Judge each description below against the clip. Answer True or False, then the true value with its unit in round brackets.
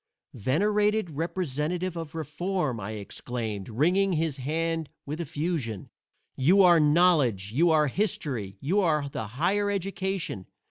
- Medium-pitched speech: True (160 Hz)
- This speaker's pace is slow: True (125 wpm)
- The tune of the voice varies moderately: False (5.7 semitones)